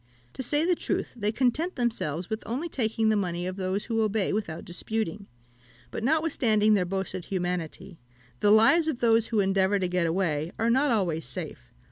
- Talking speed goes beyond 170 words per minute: Yes, average, 180 wpm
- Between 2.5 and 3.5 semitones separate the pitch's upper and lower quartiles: No, average, 4.3 semitones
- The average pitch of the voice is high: Yes, high, 210 Hz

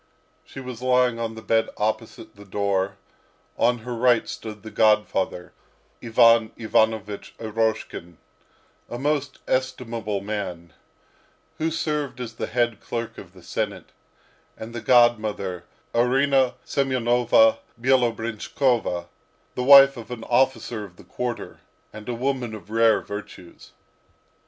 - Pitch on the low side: Yes, low, 115 Hz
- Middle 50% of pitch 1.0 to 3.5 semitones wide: Yes, average, 2.8 semitones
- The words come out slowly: Yes, slow, 125 wpm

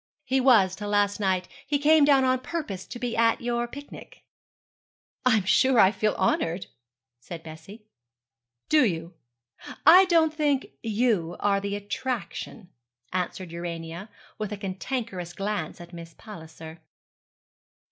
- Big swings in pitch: Yes, wide, 6.0 semitones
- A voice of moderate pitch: No, high, 205 Hz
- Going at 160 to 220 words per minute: No, slow, 135 wpm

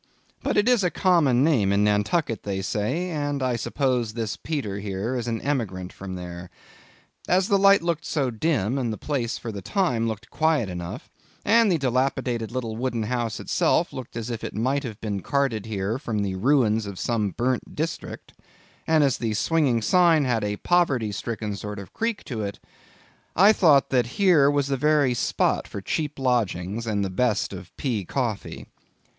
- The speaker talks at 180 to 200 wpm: Yes, average, 185 wpm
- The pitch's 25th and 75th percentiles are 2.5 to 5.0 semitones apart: No, wide, 5.6 semitones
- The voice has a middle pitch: No, low, 120 Hz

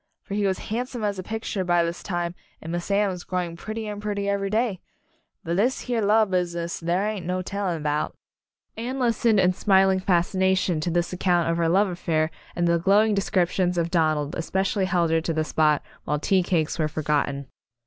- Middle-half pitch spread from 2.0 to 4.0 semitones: Yes, average, 3.1 semitones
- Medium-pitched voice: Yes, medium, 180 Hz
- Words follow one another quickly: Yes, fast, 215 wpm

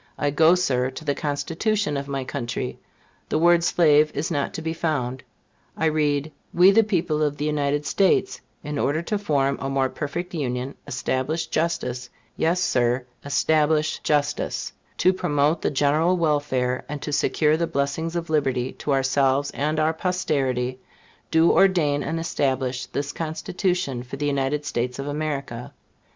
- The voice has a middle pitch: Yes, medium, 145 Hz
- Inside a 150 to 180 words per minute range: Yes, average, 160 wpm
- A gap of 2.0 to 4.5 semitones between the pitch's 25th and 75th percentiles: Yes, average, 3.0 semitones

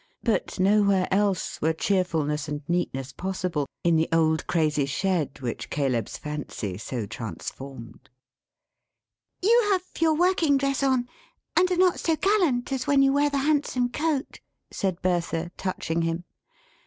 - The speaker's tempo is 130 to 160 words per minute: Yes, average, 140 wpm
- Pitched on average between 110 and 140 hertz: No, medium, 185 Hz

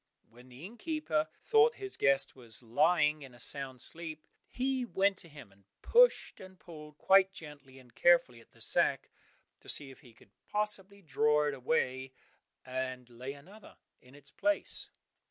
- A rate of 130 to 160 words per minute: No, average, 170 wpm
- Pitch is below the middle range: No, medium, 150 Hz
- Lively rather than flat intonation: Yes, wide, 6.8 semitones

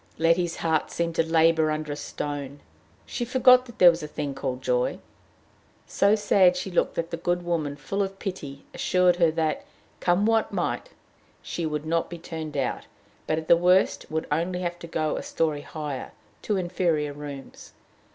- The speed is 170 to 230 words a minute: Yes, average, 180 wpm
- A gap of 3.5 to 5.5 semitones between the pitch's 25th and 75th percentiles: No, average, 3.0 semitones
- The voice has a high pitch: No, medium, 165 Hz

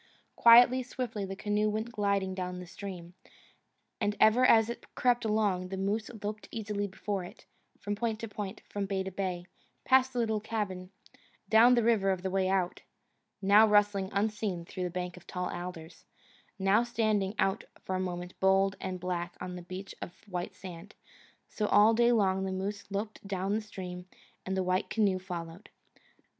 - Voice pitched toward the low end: No, high, 195 Hz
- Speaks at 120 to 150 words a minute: No, average, 180 wpm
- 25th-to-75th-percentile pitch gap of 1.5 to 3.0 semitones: Yes, average, 2.7 semitones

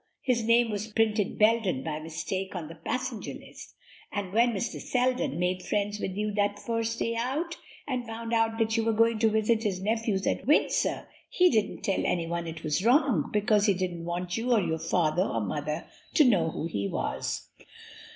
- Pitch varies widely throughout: No, average, 4.4 semitones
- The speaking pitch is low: No, high, 210 Hz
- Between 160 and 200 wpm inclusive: Yes, average, 190 wpm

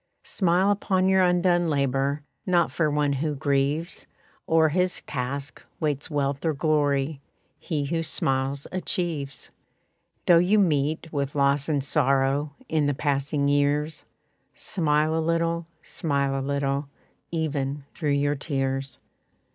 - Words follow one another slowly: Yes, slow, 130 wpm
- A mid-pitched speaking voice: Yes, medium, 145 Hz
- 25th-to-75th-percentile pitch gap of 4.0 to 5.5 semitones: No, average, 2.9 semitones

